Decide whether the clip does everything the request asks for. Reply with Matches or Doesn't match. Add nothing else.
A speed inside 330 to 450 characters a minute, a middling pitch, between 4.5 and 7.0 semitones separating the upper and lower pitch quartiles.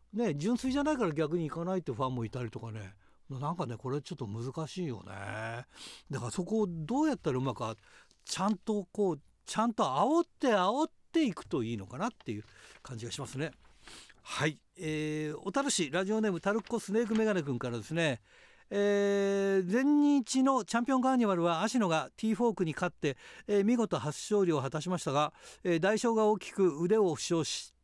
Doesn't match